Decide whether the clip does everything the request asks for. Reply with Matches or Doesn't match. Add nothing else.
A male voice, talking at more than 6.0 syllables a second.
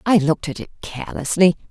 Doesn't match